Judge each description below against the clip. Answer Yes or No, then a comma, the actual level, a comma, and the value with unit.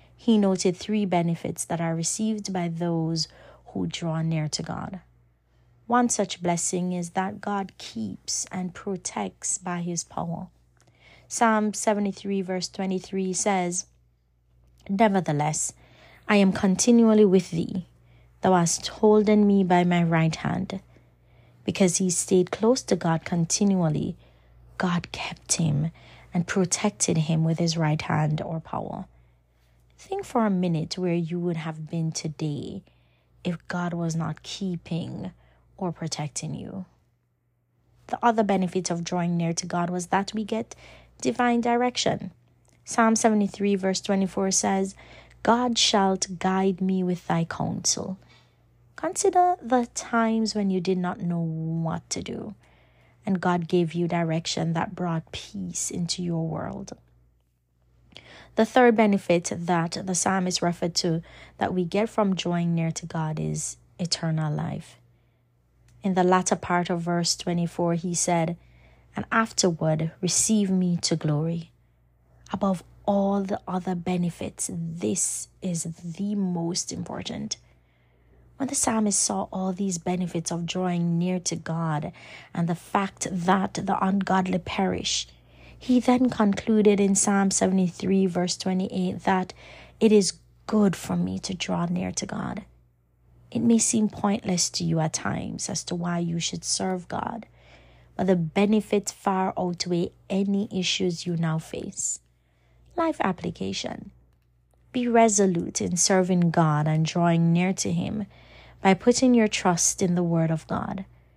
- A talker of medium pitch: Yes, medium, 175 Hz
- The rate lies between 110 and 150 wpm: Yes, average, 140 wpm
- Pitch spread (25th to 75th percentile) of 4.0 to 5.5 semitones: No, average, 3.4 semitones